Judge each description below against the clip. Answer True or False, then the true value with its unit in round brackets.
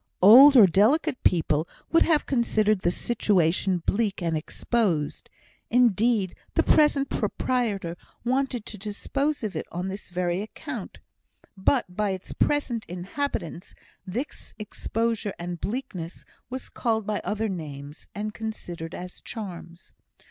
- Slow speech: True (125 wpm)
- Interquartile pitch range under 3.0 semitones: False (5.0 semitones)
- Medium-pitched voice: False (210 Hz)